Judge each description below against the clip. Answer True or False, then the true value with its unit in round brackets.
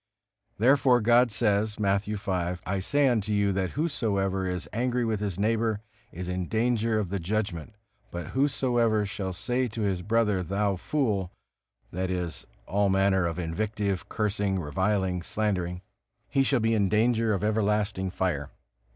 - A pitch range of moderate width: True (3.2 semitones)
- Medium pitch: False (105 Hz)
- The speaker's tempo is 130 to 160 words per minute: True (150 wpm)